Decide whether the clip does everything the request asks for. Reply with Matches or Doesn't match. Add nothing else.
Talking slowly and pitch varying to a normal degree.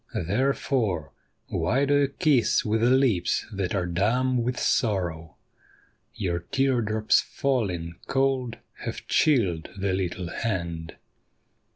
Doesn't match